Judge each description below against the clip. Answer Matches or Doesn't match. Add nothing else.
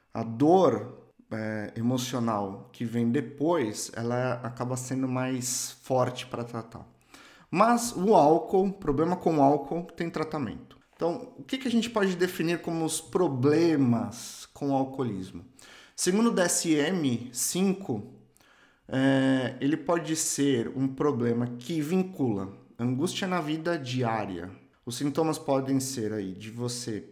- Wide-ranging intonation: Matches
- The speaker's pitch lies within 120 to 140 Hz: Matches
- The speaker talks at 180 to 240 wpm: Doesn't match